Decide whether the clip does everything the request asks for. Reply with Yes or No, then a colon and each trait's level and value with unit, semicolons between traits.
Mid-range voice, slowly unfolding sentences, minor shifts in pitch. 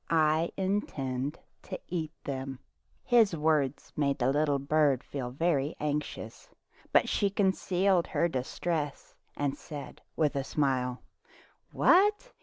No: medium, 150 Hz; slow, 125 wpm; average, 4.0 semitones